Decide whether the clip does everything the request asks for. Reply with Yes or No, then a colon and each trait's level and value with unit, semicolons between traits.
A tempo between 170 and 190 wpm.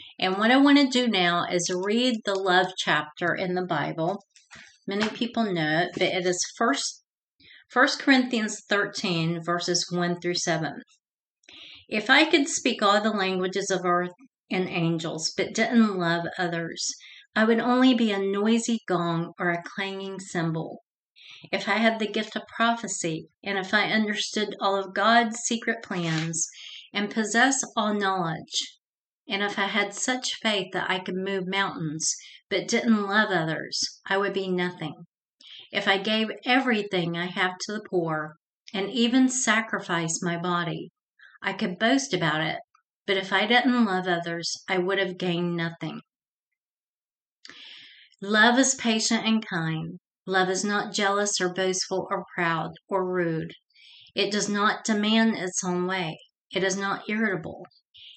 No: average, 155 wpm